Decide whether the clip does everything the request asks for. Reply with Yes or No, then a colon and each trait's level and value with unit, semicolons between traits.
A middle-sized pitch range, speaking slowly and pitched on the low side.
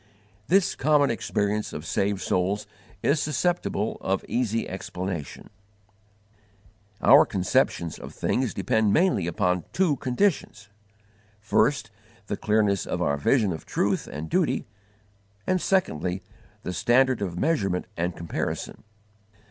No: wide, 6.7 semitones; slow, 115 wpm; low, 105 Hz